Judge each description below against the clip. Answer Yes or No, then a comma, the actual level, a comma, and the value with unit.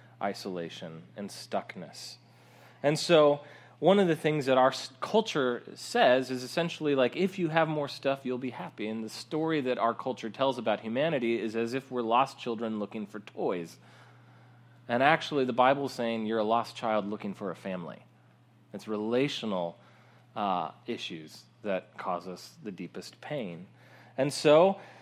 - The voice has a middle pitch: No, low, 125 Hz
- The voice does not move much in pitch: No, average, 4.5 semitones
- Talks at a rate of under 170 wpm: Yes, average, 160 wpm